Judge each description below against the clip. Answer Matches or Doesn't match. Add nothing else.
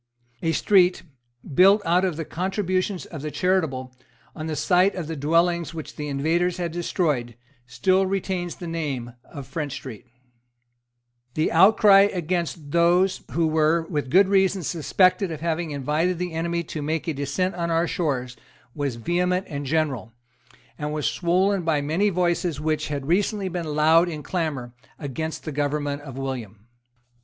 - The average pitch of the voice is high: Doesn't match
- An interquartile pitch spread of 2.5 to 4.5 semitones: Matches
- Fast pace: Doesn't match